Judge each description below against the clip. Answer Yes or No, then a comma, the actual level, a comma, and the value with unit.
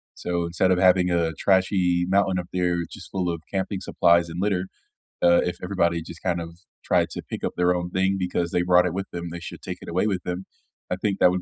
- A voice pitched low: Yes, very low, 90 Hz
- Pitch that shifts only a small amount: Yes, narrow, 1.4 semitones